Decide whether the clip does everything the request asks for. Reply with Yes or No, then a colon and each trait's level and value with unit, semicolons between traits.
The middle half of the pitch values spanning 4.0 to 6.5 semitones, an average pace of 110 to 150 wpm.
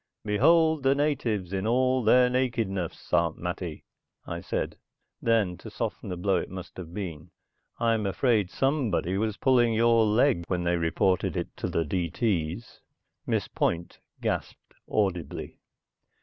Yes: average, 5.3 semitones; average, 140 wpm